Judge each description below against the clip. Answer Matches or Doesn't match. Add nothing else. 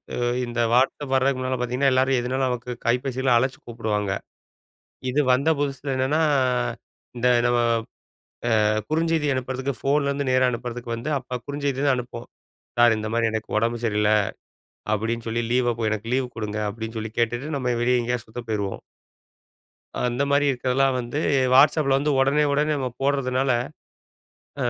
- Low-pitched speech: Matches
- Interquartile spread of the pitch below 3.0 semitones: Matches